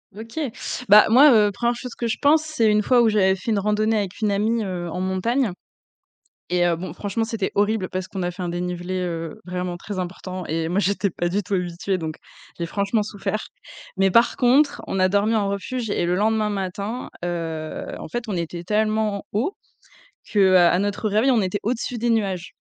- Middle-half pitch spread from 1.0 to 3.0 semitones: No, average, 3.4 semitones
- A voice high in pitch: Yes, high, 200 Hz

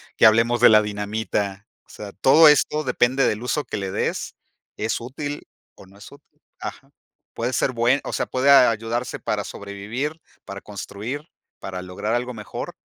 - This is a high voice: No, low, 115 Hz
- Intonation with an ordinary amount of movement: Yes, average, 4.2 semitones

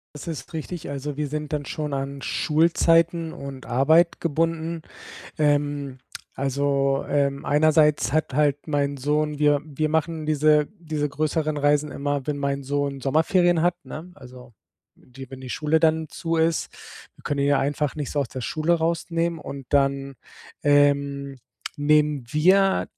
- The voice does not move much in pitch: Yes, narrow, 2.2 semitones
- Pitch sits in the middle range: Yes, medium, 145 Hz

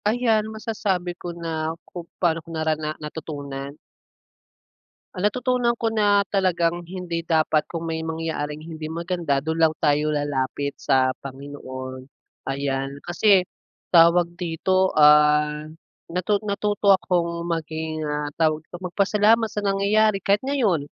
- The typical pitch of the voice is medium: Yes, medium, 165 Hz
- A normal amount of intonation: Yes, average, 4.2 semitones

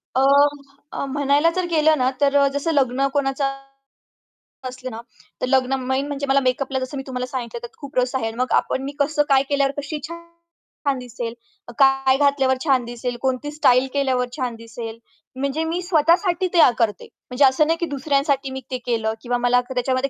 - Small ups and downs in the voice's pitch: Yes, narrow, 2.3 semitones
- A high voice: Yes, very high, 270 Hz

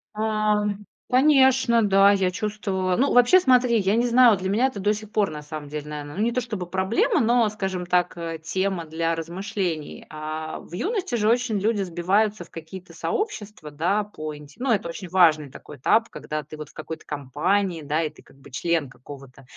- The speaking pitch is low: No, high, 190 Hz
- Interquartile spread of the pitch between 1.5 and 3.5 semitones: No, wide, 5.6 semitones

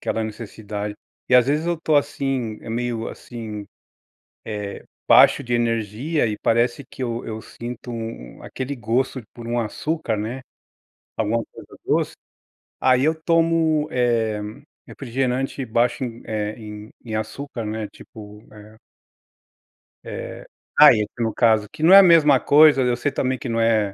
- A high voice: No, low, 120 Hz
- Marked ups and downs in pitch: No, average, 3.6 semitones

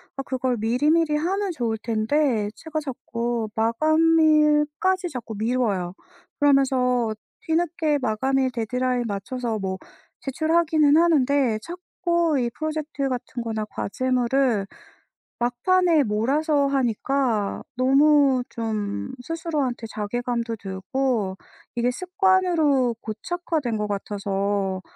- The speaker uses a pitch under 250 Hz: No, very high, 255 Hz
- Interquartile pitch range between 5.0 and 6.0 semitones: Yes, wide, 5.4 semitones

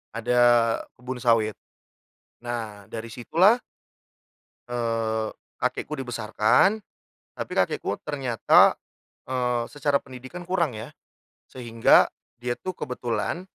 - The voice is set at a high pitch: No, low, 120 Hz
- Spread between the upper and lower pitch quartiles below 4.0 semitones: Yes, average, 3.0 semitones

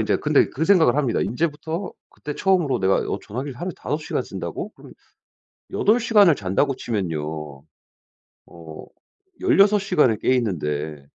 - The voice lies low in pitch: Yes, low, 130 Hz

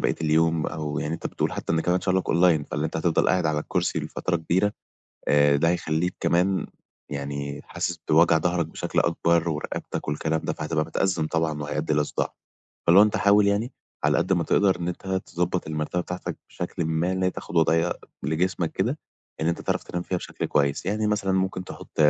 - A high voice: No, very low, 85 Hz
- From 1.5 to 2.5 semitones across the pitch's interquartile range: No, average, 2.9 semitones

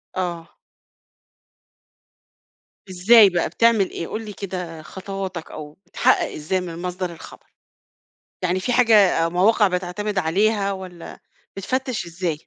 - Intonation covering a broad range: No, average, 3.1 semitones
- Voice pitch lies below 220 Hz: Yes, medium, 185 Hz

